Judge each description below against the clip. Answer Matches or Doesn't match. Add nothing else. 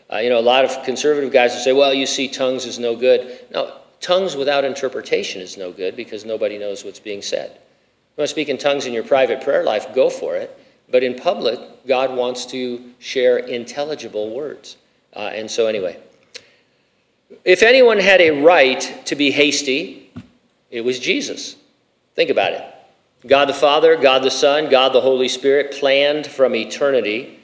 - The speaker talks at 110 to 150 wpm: Doesn't match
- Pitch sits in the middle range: Matches